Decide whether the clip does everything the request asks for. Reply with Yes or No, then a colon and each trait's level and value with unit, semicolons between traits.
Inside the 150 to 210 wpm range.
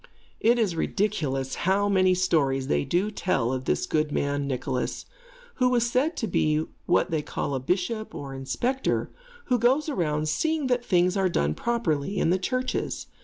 Yes: average, 170 wpm